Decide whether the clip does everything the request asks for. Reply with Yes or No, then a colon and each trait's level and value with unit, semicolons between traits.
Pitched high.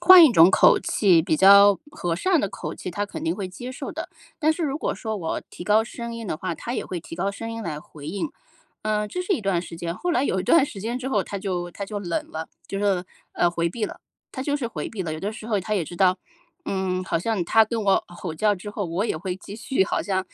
Yes: high, 200 Hz